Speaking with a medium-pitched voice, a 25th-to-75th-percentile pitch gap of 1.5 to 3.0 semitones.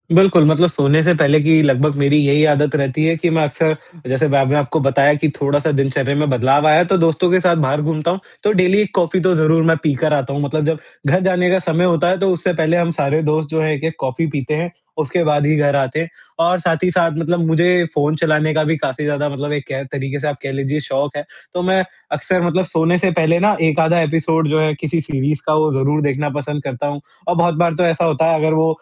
Yes: medium, 155 Hz; narrow, 2.5 semitones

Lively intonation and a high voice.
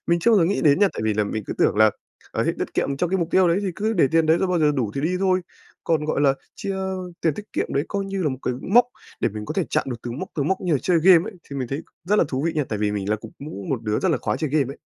No: wide, 6.1 semitones; medium, 155 Hz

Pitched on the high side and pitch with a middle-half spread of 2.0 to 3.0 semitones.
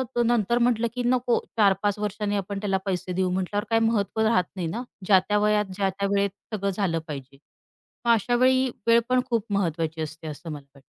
No: high, 200 Hz; average, 3.9 semitones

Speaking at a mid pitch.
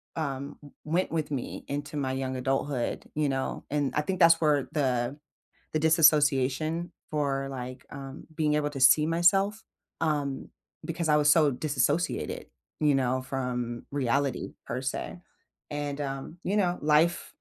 Yes: medium, 145 Hz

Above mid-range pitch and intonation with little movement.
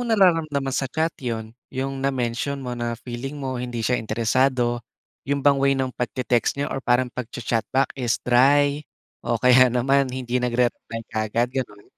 No: low, 125 Hz; narrow, 2.3 semitones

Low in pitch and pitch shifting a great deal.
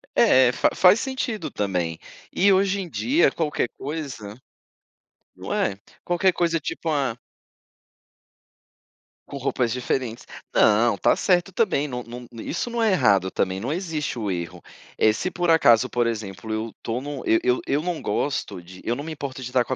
Yes: low, 130 Hz; wide, 7.2 semitones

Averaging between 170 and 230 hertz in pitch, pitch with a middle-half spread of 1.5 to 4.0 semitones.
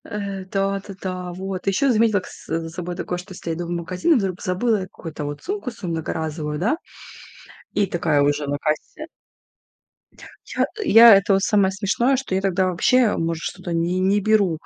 Yes: medium, 185 Hz; average, 3.5 semitones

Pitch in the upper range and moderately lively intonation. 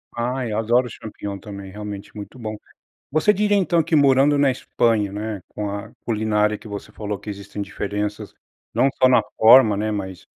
No: low, 110 Hz; average, 3.9 semitones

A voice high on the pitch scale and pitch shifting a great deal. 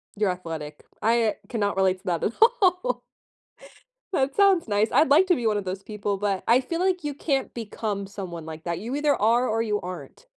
Yes: high, 215 Hz; wide, 6.7 semitones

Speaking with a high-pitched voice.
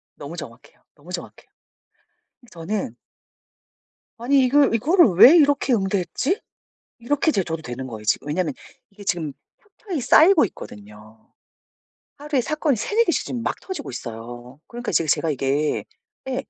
Yes: high, 210 Hz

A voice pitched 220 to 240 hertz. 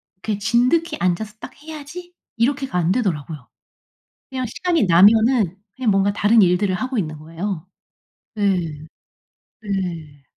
No: high, 205 Hz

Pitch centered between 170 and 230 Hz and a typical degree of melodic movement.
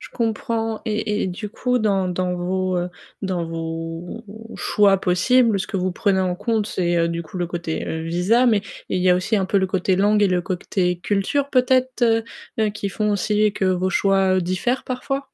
Yes: high, 190 Hz; average, 3.4 semitones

